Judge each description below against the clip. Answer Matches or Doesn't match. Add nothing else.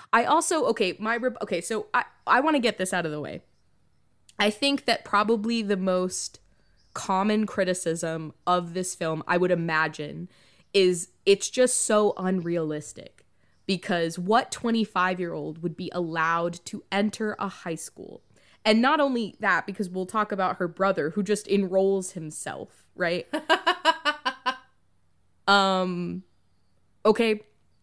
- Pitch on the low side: Doesn't match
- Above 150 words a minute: Doesn't match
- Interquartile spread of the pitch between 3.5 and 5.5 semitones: Matches